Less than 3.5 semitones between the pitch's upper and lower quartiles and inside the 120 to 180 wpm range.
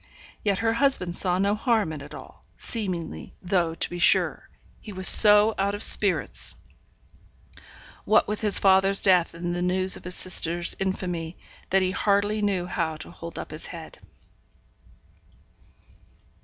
Yes: average, 2.9 semitones; average, 155 wpm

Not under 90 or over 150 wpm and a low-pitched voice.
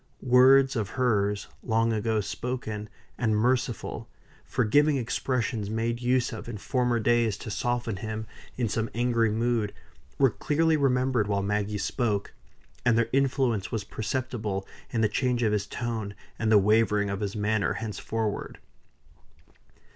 Yes: average, 140 wpm; low, 115 Hz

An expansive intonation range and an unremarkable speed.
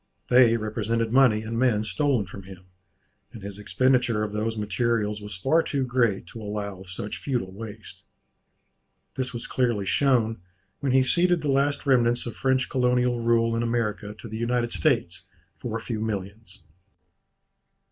No: average, 3.2 semitones; average, 160 wpm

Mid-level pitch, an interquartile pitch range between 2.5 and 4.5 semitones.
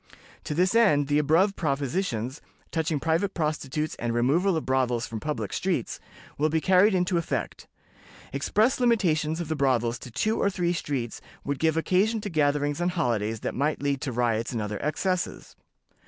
No: medium, 150 Hz; average, 5.3 semitones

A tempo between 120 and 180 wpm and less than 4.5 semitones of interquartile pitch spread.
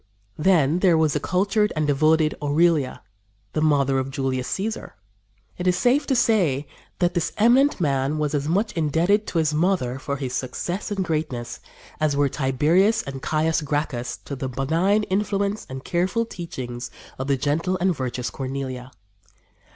No: average, 165 wpm; average, 5.3 semitones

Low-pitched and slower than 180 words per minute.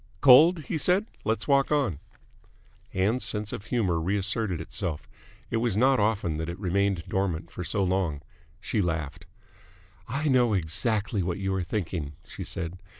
Yes: low, 100 Hz; average, 155 wpm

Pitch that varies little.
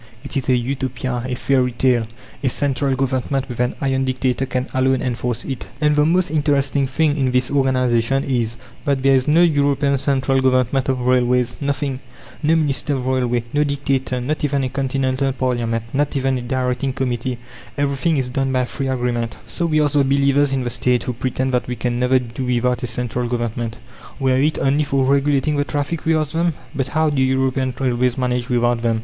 Yes: narrow, 1.9 semitones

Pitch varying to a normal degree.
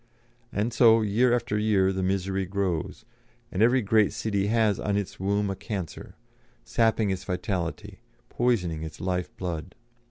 Yes: average, 3.0 semitones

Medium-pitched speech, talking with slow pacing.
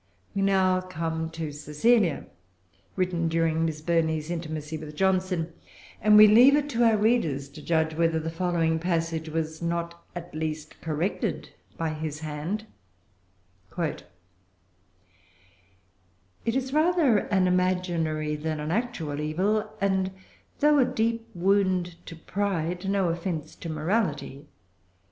Yes: medium, 170 Hz; slow, 125 wpm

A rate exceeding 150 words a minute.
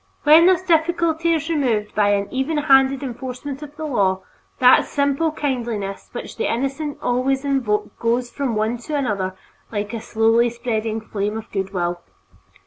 Yes: average, 160 wpm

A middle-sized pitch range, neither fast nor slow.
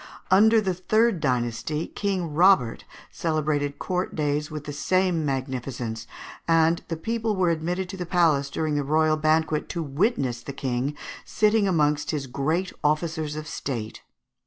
Yes: average, 4.1 semitones; average, 150 wpm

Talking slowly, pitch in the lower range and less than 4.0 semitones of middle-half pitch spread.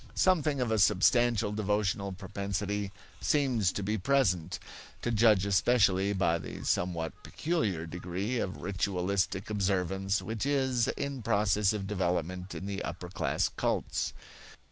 Yes: slow, 130 wpm; low, 100 Hz; average, 3.3 semitones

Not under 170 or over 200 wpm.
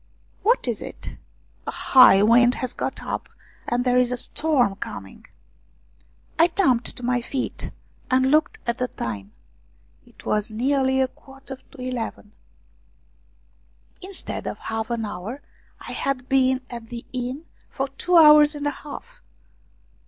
No: average, 155 wpm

